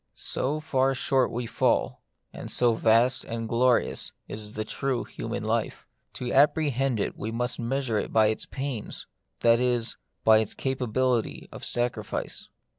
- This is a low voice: Yes, low, 120 Hz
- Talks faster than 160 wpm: No, average, 155 wpm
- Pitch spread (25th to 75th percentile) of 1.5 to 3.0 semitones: Yes, average, 2.7 semitones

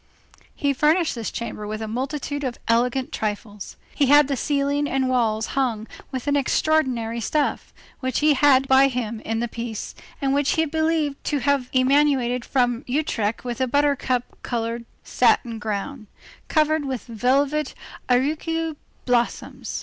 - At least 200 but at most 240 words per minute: No, average, 150 wpm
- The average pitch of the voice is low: No, very high, 260 Hz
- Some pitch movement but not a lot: Yes, average, 3.4 semitones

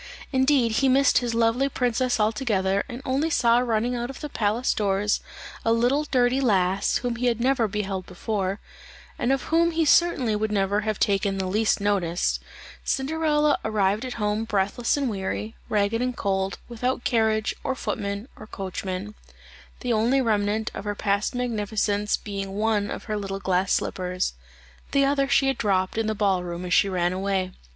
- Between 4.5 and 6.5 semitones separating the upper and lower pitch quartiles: No, average, 3.9 semitones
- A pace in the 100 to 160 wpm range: No, average, 175 wpm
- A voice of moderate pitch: No, high, 215 Hz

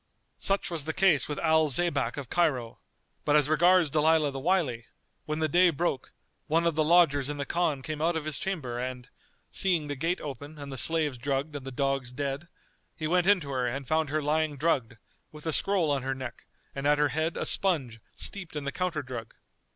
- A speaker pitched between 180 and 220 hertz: No, medium, 150 Hz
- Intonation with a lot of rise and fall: No, average, 3.2 semitones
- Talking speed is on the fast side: Yes, fast, 215 wpm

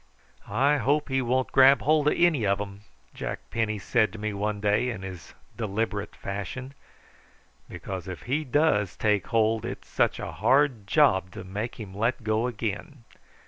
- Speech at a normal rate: Yes, average, 170 wpm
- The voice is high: No, low, 110 Hz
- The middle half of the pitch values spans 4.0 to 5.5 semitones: Yes, average, 4.4 semitones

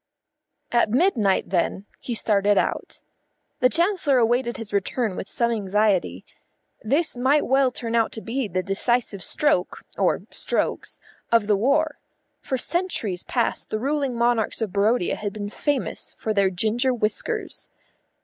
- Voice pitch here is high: Yes, high, 230 Hz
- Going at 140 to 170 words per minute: Yes, average, 145 wpm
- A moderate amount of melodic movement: Yes, average, 4.3 semitones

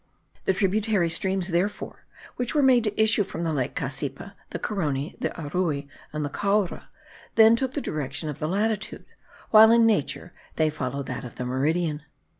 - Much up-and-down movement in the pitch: Yes, wide, 6.4 semitones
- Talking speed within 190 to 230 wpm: No, average, 175 wpm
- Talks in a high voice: No, medium, 175 Hz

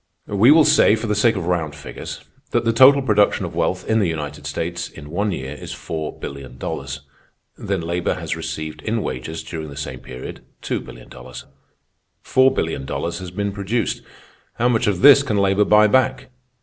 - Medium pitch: No, very low, 95 Hz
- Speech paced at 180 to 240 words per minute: Yes, average, 190 wpm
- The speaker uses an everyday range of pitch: No, wide, 6.3 semitones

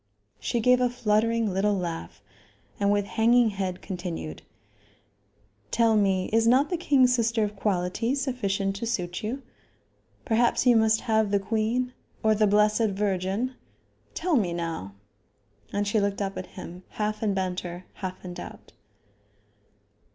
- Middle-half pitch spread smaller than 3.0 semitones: No, average, 3.4 semitones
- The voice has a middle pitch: No, high, 210 Hz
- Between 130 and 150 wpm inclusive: Yes, average, 145 wpm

